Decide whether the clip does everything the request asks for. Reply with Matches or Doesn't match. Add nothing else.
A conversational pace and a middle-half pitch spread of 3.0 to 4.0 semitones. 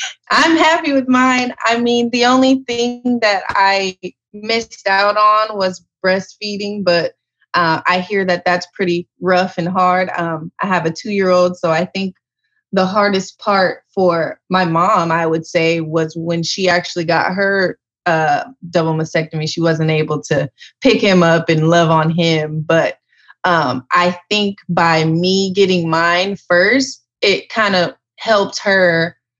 Matches